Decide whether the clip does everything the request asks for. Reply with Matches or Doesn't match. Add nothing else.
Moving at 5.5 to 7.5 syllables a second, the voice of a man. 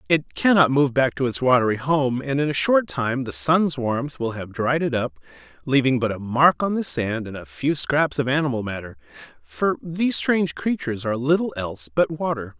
Doesn't match